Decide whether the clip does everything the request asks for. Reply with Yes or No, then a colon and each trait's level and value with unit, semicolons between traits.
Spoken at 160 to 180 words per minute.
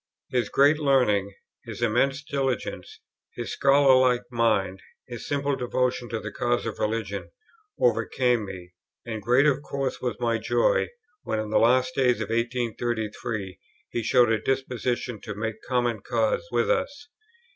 No: average, 145 wpm